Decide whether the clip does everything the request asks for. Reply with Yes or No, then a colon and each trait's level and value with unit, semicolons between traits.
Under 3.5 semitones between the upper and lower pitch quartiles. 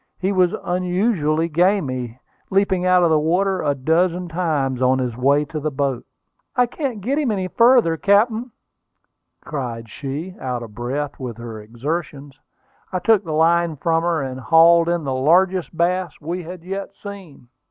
No: average, 5.1 semitones